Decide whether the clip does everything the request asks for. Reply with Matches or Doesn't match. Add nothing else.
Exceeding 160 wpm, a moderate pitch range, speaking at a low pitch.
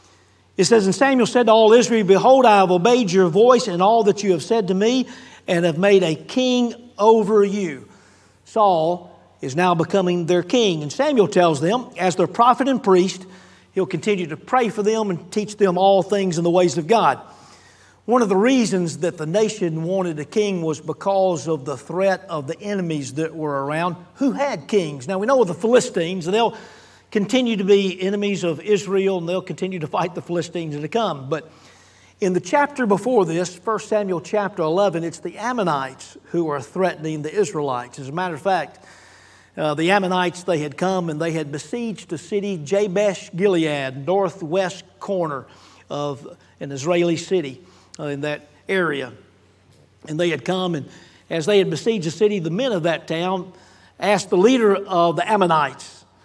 Doesn't match